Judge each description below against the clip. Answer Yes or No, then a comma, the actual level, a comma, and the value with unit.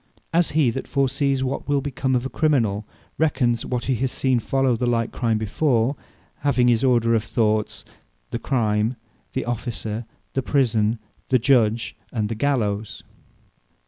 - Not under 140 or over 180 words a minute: Yes, average, 165 wpm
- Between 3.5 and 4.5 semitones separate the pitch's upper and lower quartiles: No, average, 3.1 semitones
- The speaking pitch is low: Yes, low, 120 Hz